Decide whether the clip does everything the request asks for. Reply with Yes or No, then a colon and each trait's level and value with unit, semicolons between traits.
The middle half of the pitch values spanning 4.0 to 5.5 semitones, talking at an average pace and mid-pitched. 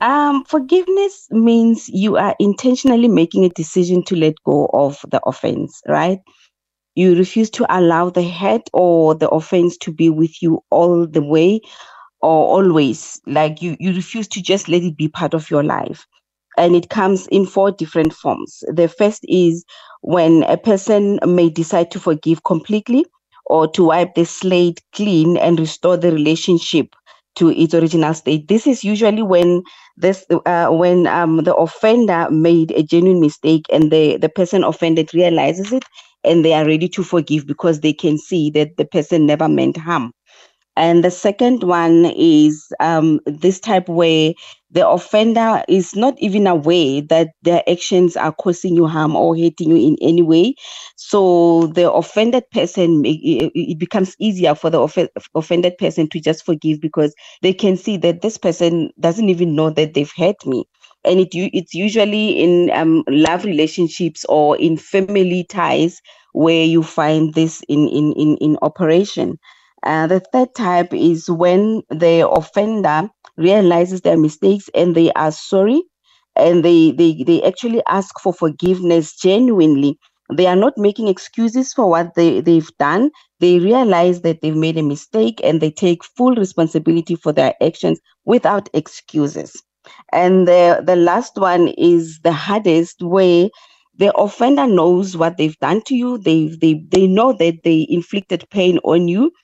No: average, 3.4 semitones; average, 165 wpm; medium, 175 Hz